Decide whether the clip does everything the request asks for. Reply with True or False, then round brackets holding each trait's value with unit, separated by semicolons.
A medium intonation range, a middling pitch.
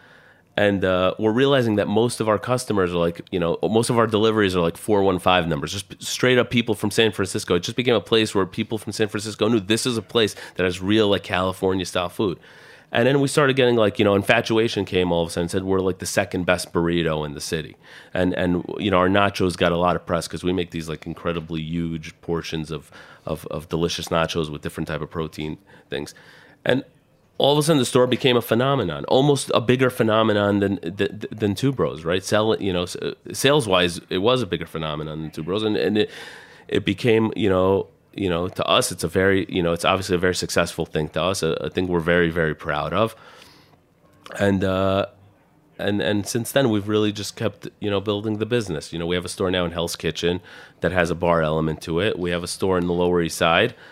False (4.2 semitones; 95 Hz)